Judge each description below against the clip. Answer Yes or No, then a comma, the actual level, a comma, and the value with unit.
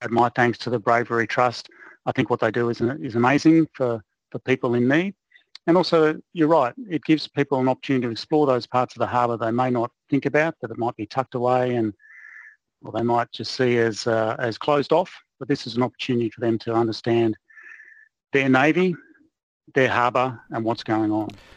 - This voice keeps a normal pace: No, fast, 210 wpm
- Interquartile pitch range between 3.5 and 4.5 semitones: Yes, average, 3.8 semitones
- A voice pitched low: Yes, low, 125 Hz